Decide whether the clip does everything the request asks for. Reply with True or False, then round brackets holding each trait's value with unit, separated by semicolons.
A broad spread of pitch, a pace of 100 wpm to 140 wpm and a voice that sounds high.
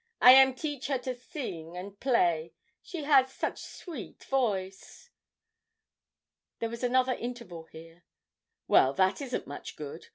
True (6.9 semitones; 135 wpm; 240 Hz)